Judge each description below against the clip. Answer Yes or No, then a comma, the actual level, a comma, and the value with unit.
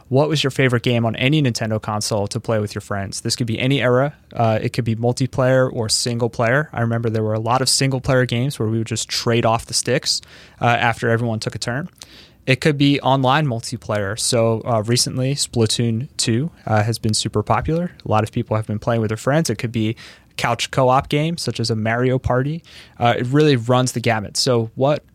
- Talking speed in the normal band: No, fast, 230 wpm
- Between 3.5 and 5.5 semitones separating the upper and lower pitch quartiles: No, narrow, 2.6 semitones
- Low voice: Yes, low, 120 Hz